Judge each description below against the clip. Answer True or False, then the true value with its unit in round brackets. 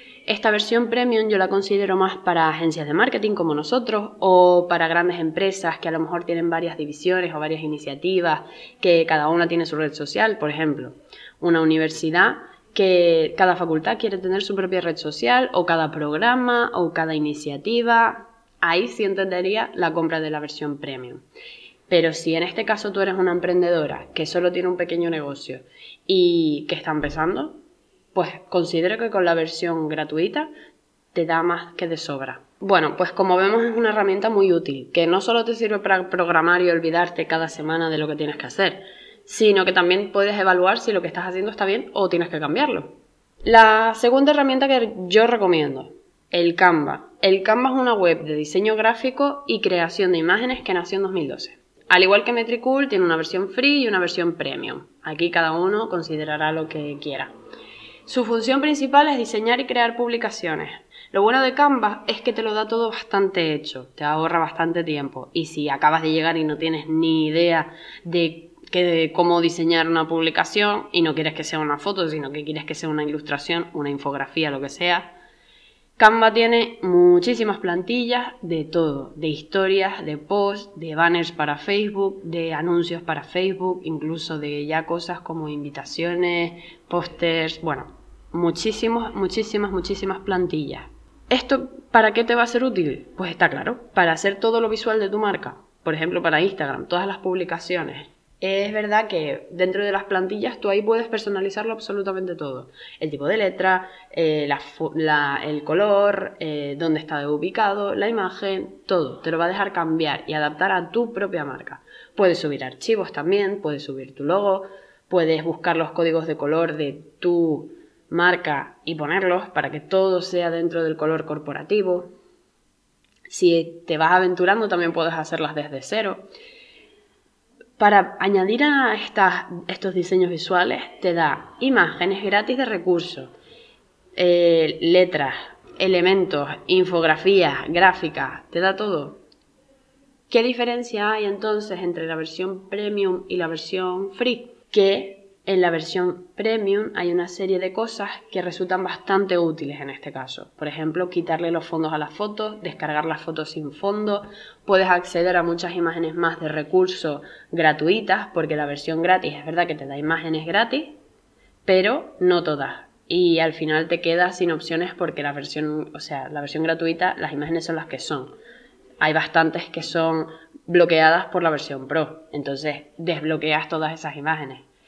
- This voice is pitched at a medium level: True (175 Hz)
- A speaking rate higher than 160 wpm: True (170 wpm)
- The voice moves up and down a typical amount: True (4.0 semitones)